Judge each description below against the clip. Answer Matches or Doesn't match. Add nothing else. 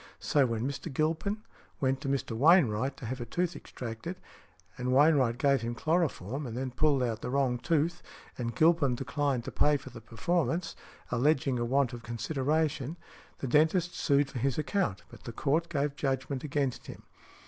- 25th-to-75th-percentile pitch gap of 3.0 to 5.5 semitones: Matches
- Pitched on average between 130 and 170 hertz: Matches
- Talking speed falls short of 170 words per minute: Doesn't match